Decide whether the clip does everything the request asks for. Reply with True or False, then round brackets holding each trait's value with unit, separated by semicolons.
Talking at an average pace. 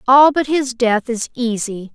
True (185 wpm)